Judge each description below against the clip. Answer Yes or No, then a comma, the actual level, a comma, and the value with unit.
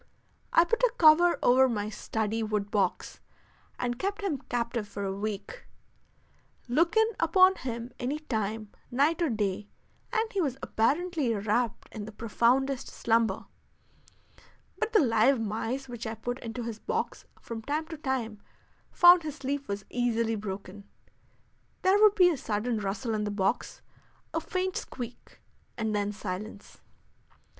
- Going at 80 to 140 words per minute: No, average, 150 wpm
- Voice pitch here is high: Yes, high, 240 Hz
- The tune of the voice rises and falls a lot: Yes, wide, 6.3 semitones